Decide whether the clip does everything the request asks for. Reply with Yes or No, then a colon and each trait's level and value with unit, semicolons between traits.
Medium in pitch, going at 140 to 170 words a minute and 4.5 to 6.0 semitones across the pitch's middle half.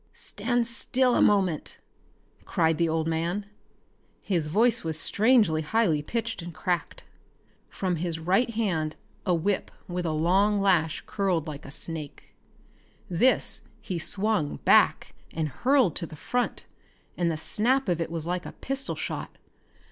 Yes: medium, 180 Hz; average, 150 wpm; average, 5.1 semitones